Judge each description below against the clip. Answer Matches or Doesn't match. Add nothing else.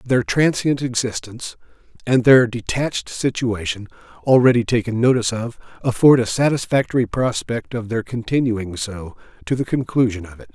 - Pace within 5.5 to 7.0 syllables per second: Doesn't match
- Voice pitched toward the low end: Matches